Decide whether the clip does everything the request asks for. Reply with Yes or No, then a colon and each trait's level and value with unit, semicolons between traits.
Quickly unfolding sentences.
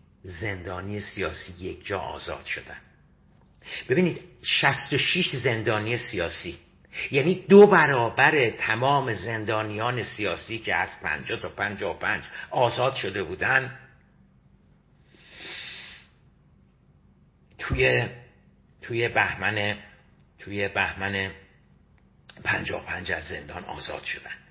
No: slow, 85 wpm